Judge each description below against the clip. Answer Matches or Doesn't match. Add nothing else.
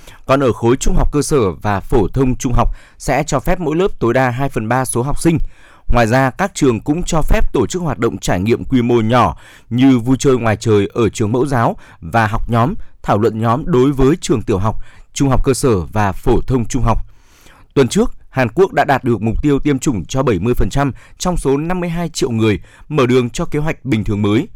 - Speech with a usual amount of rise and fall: Matches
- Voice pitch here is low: Matches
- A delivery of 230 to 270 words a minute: Matches